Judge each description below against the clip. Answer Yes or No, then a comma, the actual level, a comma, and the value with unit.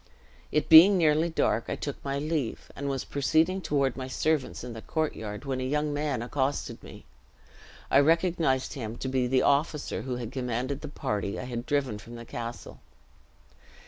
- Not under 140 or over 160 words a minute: No, average, 175 wpm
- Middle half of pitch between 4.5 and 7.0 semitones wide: No, average, 3.5 semitones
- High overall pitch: No, low, 135 Hz